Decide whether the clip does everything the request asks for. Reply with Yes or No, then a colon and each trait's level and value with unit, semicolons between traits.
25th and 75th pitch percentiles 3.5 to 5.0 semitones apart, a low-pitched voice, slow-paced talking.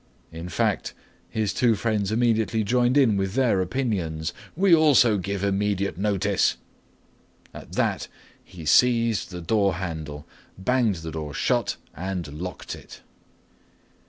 Yes: average, 4.7 semitones; low, 100 Hz; slow, 130 wpm